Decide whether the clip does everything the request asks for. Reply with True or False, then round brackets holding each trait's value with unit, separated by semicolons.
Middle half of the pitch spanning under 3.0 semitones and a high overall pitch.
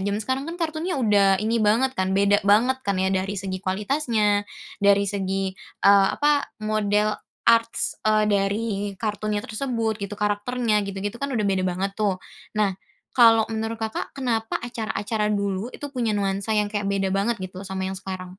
True (2.6 semitones; 210 Hz)